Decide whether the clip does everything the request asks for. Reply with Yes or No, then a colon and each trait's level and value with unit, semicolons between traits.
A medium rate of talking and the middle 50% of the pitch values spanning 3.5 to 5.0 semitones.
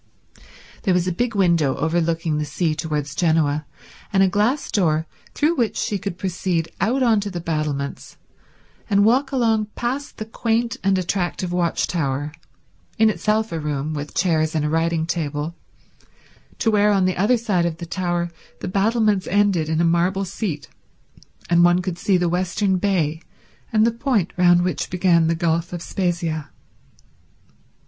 Yes: average, 165 wpm; average, 4.0 semitones